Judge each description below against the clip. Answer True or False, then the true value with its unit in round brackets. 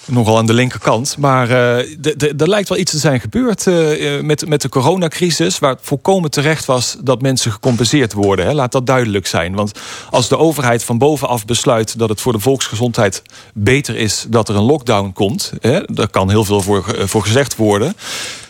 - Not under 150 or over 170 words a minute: False (200 wpm)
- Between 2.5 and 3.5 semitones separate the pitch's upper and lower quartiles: False (5.1 semitones)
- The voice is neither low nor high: False (125 Hz)